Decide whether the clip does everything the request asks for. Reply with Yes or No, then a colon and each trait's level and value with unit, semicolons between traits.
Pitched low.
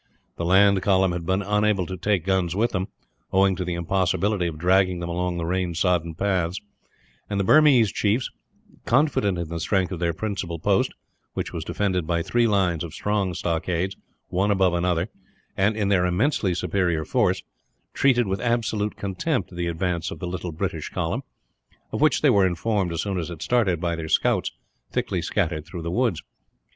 Yes: very low, 95 Hz